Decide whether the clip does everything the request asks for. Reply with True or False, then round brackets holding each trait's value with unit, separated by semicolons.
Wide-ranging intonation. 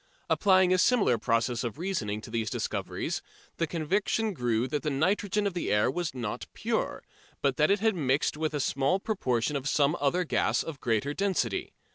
True (7.1 semitones)